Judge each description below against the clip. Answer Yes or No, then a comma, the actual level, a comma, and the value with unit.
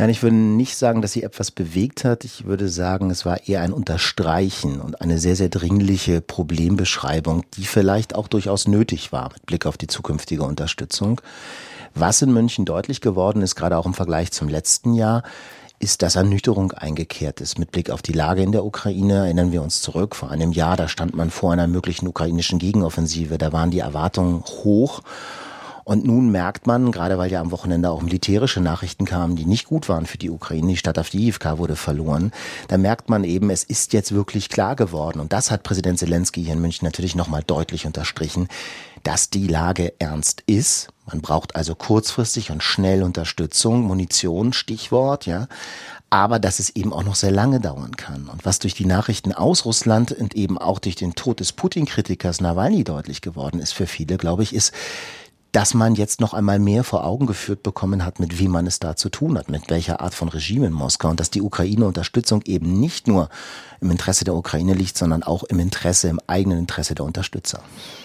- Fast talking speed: Yes, fast, 200 wpm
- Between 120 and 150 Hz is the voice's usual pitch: No, very low, 95 Hz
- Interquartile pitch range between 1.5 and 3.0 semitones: No, average, 3.9 semitones